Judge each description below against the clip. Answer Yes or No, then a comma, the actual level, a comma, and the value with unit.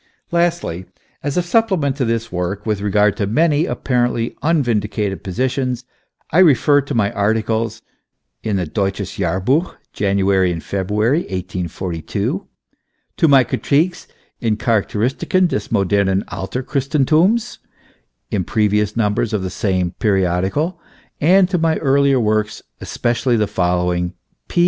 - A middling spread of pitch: No, wide, 6.4 semitones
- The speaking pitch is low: Yes, low, 110 Hz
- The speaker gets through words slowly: Yes, slow, 130 wpm